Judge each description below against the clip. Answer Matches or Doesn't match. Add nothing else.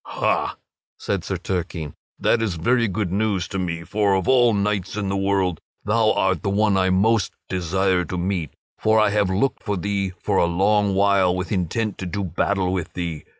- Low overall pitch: Matches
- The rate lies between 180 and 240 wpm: Matches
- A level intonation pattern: Matches